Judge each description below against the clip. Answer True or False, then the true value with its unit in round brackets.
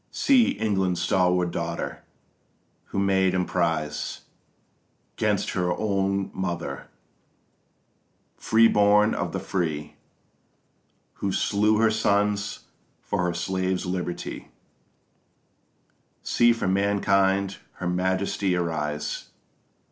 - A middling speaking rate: False (90 wpm)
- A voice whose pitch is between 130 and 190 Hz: False (95 Hz)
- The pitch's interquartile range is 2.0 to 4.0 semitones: True (2.5 semitones)